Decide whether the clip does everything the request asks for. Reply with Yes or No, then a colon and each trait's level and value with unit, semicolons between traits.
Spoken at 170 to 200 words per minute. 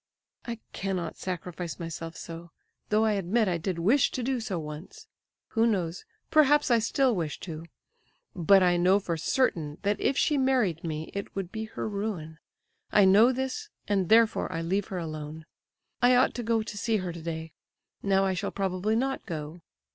Yes: average, 180 wpm